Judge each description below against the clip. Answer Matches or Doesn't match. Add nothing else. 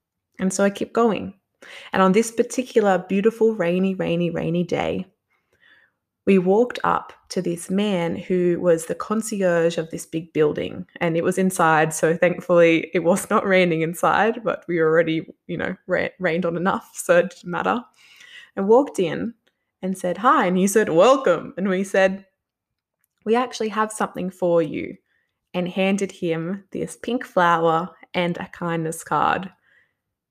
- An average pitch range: Matches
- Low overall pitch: Doesn't match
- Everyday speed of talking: Matches